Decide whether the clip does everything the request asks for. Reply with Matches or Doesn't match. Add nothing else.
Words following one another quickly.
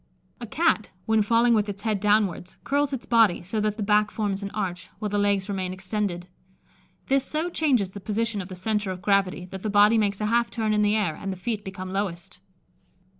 Matches